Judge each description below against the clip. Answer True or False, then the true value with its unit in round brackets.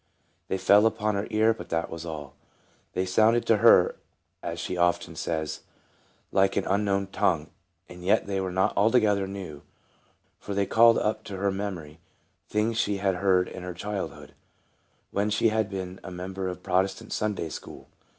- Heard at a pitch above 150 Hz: False (95 Hz)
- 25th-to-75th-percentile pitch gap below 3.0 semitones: True (2.6 semitones)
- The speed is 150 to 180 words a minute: True (175 wpm)